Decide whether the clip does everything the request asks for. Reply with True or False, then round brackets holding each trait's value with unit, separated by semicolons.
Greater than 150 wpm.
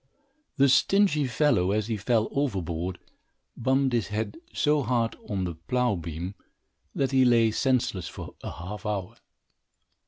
False (145 wpm)